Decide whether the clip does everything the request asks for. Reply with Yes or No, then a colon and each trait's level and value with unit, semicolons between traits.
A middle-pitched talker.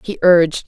Yes: medium, 175 Hz